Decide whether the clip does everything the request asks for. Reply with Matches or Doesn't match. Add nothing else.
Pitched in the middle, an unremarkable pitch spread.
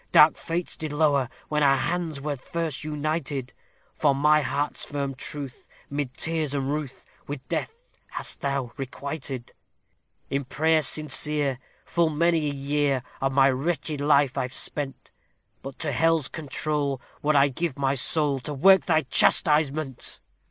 Doesn't match